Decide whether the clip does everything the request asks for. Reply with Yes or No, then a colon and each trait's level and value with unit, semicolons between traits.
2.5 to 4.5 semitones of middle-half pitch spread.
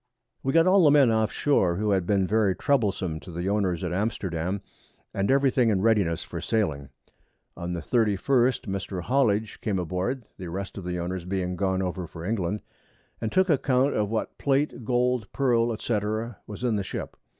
No: average, 5.0 semitones